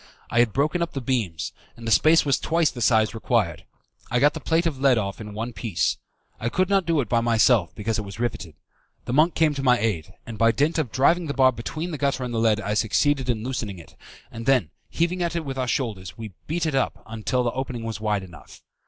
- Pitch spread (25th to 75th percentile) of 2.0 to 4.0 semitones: No, average, 4.8 semitones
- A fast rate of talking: Yes, fast, 245 wpm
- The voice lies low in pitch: Yes, low, 125 Hz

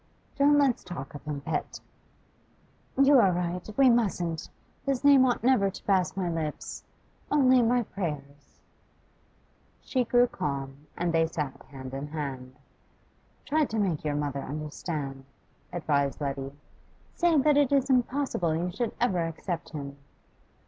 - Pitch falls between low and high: Yes, medium, 175 Hz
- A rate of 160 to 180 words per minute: No, average, 150 wpm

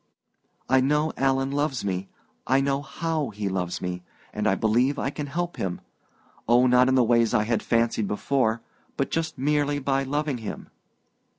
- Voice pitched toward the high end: No, low, 130 Hz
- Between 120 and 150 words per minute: No, average, 175 wpm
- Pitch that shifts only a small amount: No, average, 4.2 semitones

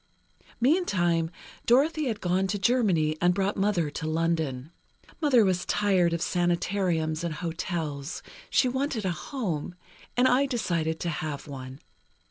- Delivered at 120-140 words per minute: Yes, slow, 135 wpm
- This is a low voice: No, medium, 175 Hz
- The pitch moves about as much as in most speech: Yes, average, 5.0 semitones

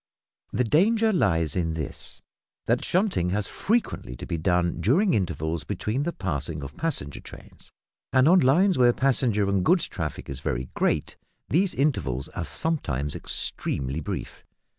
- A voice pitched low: Yes, low, 100 Hz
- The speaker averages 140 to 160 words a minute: Yes, average, 150 wpm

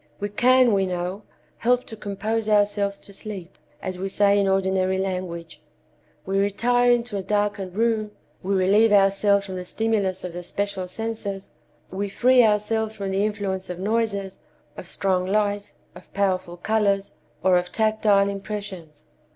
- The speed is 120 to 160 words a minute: Yes, average, 155 wpm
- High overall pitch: Yes, high, 200 Hz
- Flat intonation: Yes, narrow, 2.1 semitones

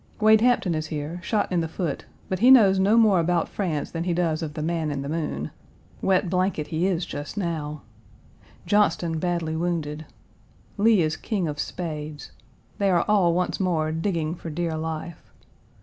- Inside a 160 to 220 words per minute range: Yes, average, 180 wpm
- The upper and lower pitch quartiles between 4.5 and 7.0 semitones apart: No, average, 3.2 semitones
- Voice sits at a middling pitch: Yes, medium, 170 Hz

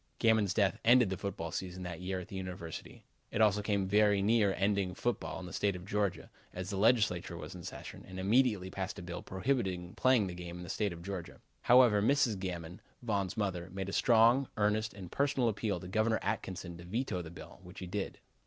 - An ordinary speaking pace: No, fast, 210 wpm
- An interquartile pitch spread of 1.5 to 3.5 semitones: Yes, average, 3.1 semitones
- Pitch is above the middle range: No, very low, 95 Hz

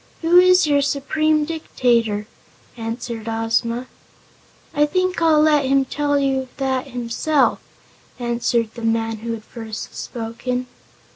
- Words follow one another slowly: Yes, slow, 125 wpm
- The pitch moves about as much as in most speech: Yes, average, 4.4 semitones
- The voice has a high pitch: Yes, very high, 255 Hz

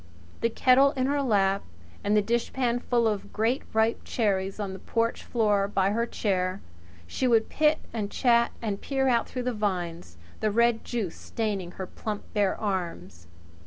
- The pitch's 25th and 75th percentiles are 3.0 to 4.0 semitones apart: Yes, average, 3.4 semitones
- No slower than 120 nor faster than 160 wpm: No, average, 170 wpm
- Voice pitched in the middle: No, high, 215 Hz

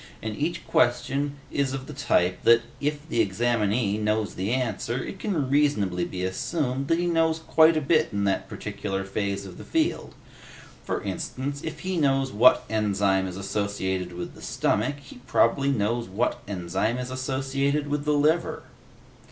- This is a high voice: No, low, 125 Hz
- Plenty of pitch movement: Yes, wide, 6.3 semitones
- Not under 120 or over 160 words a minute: No, average, 170 wpm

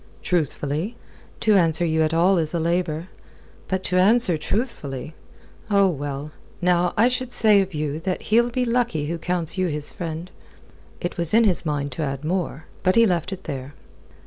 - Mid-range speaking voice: Yes, medium, 175 Hz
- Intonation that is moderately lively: Yes, average, 4.0 semitones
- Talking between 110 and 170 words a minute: No, average, 180 wpm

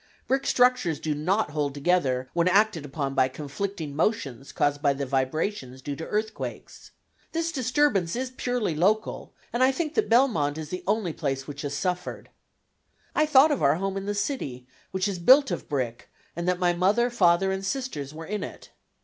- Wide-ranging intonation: Yes, wide, 7.5 semitones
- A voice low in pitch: No, medium, 180 Hz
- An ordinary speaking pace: Yes, average, 185 wpm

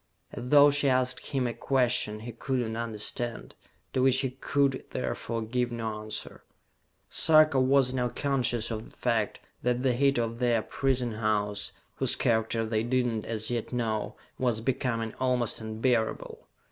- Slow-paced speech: No, average, 160 wpm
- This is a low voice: Yes, low, 120 Hz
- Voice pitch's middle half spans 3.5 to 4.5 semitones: No, narrow, 2.5 semitones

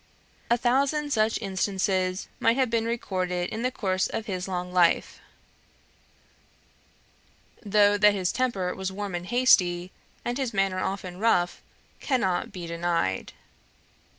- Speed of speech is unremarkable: No, slow, 130 wpm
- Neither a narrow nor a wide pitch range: Yes, average, 4.1 semitones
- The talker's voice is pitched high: Yes, high, 195 Hz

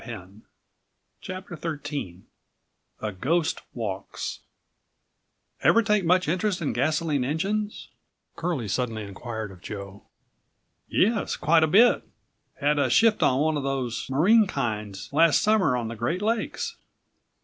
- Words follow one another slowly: Yes, slow, 125 wpm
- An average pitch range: No, wide, 8.0 semitones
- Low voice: No, medium, 145 Hz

